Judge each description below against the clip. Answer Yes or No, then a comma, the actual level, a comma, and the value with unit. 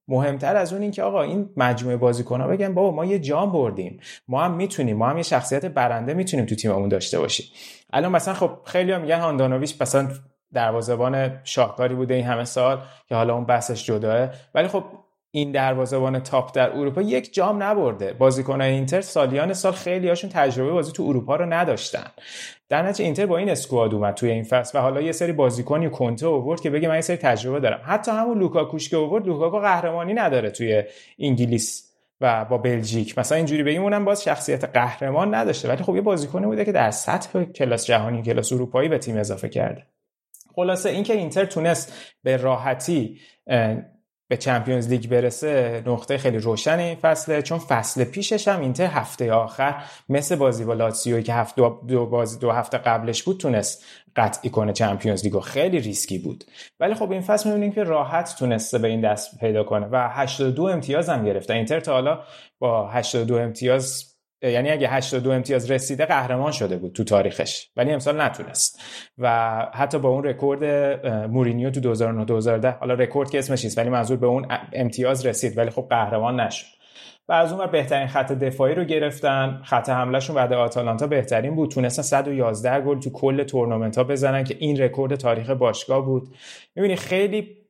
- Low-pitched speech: Yes, low, 130 Hz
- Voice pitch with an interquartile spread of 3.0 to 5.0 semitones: Yes, average, 4.7 semitones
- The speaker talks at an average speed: No, fast, 180 wpm